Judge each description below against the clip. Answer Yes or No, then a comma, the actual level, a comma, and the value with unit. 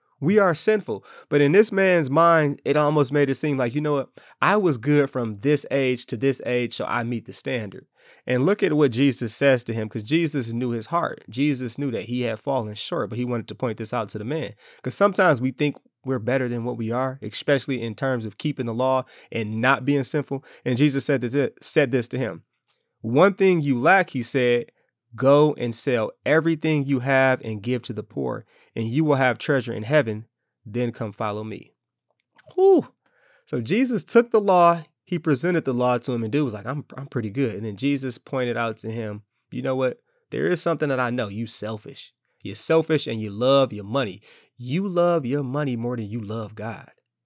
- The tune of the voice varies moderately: Yes, average, 4.0 semitones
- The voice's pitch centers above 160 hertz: No, low, 130 Hz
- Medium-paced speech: No, fast, 215 wpm